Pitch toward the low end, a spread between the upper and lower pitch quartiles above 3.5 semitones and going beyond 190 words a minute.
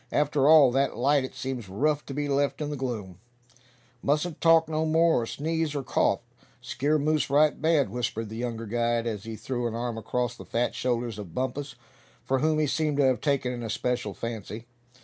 Yes: low, 130 Hz; average, 4.1 semitones; average, 200 wpm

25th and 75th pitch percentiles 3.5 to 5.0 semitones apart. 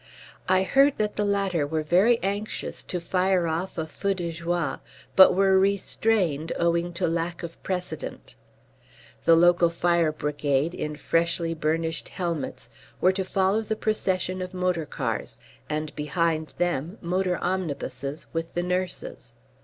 No: average, 2.8 semitones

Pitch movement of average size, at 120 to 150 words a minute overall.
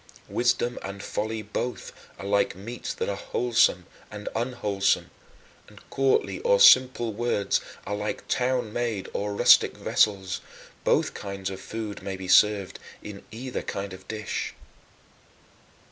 Yes: average, 3.5 semitones; slow, 135 wpm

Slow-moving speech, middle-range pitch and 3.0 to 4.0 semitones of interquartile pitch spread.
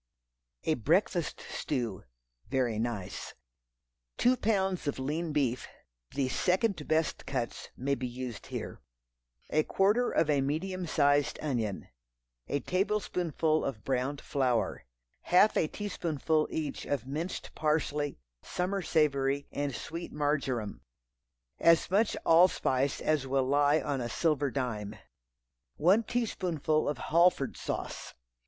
No: slow, 120 wpm; medium, 150 Hz; average, 4.4 semitones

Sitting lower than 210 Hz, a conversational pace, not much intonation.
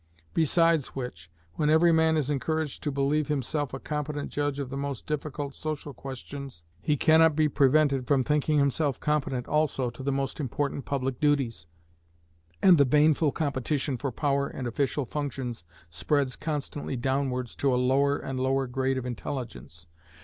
Yes: medium, 140 Hz; average, 160 wpm; narrow, 2.3 semitones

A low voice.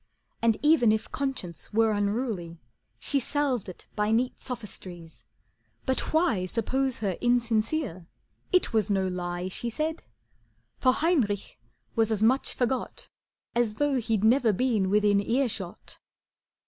No: high, 225 Hz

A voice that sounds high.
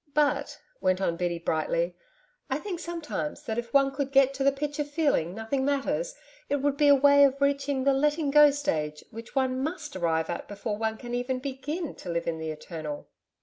Yes: very high, 270 Hz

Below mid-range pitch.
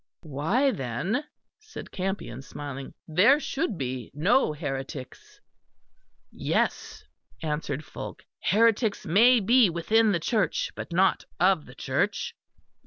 No: medium, 185 Hz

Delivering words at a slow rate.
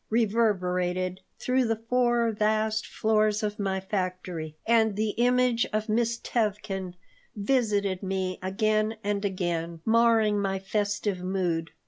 Yes: slow, 120 wpm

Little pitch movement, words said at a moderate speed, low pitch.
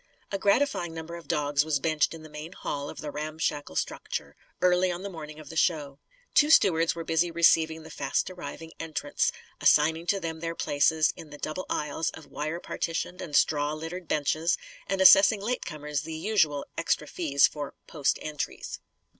No: narrow, 2.3 semitones; average, 180 wpm; medium, 160 Hz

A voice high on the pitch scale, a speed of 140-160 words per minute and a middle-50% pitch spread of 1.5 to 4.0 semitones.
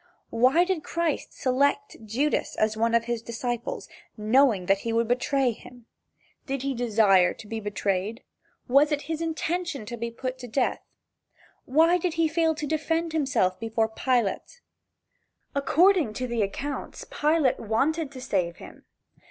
No: very high, 255 Hz; average, 150 wpm; average, 5.2 semitones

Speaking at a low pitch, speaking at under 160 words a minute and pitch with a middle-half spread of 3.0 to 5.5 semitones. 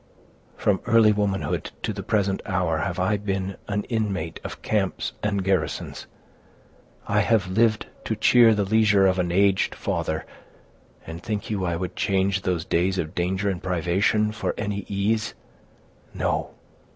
No: low, 100 Hz; average, 150 wpm; narrow, 2.4 semitones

